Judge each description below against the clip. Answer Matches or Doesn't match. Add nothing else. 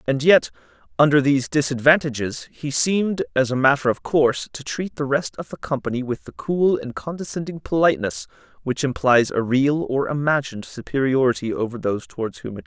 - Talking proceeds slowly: Doesn't match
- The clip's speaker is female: Doesn't match